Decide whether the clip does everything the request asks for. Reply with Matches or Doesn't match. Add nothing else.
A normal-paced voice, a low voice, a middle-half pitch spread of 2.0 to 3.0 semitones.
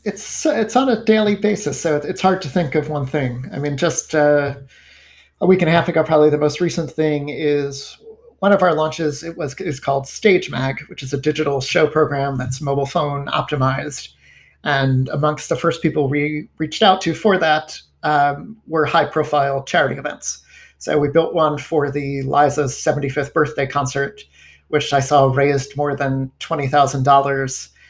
Doesn't match